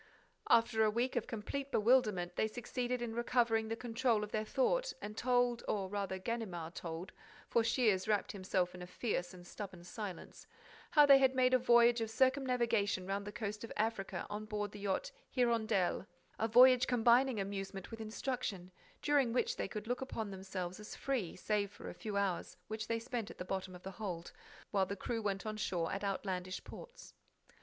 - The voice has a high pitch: Yes, high, 215 Hz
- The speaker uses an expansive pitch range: No, average, 3.8 semitones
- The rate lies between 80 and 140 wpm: No, average, 185 wpm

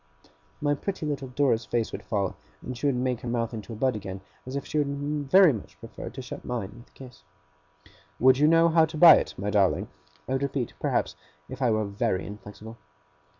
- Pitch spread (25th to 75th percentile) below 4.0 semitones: No, average, 4.4 semitones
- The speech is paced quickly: Yes, fast, 215 wpm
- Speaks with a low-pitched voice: Yes, low, 125 Hz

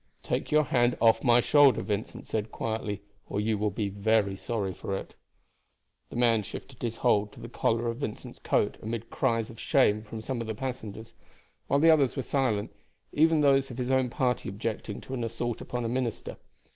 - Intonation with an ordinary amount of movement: Yes, average, 3.1 semitones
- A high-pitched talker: No, low, 115 Hz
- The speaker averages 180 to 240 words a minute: Yes, average, 195 wpm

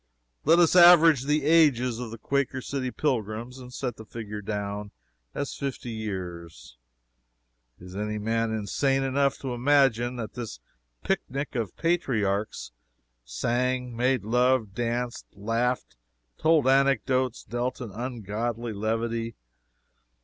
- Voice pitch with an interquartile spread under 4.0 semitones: Yes, average, 3.5 semitones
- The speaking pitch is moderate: No, low, 120 Hz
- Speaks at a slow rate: Yes, slow, 120 wpm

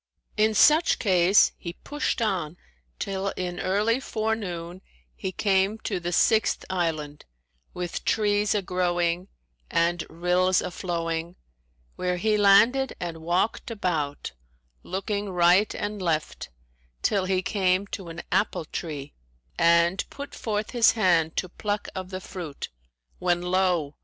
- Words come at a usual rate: No, slow, 130 wpm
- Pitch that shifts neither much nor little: Yes, average, 3.1 semitones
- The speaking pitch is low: No, medium, 185 Hz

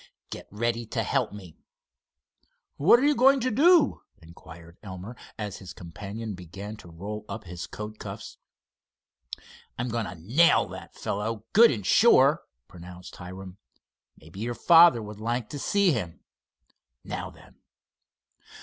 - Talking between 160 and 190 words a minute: No, average, 140 wpm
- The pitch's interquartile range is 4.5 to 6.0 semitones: Yes, average, 5.1 semitones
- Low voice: Yes, low, 105 Hz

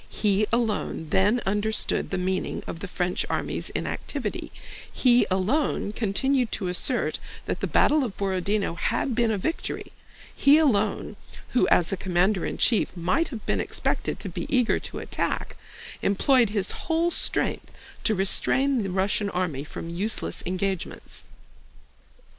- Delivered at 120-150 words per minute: Yes, slow, 135 wpm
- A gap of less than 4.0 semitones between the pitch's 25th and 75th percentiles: No, average, 4.5 semitones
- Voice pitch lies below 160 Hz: No, high, 205 Hz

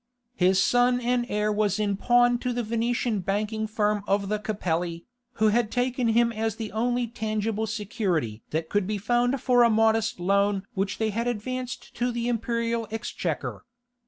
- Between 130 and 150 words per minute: No, average, 170 wpm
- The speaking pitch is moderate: No, high, 220 Hz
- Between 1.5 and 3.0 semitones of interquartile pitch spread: Yes, average, 2.7 semitones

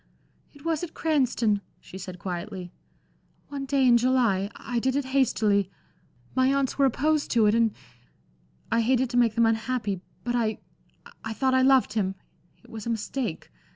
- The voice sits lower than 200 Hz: No, high, 240 Hz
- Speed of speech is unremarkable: Yes, average, 170 wpm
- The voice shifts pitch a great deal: No, average, 3.7 semitones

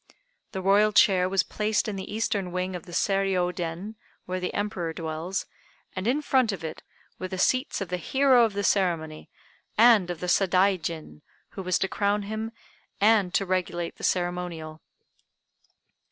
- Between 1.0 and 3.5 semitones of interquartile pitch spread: Yes, average, 2.8 semitones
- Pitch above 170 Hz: Yes, high, 190 Hz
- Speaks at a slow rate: No, average, 170 wpm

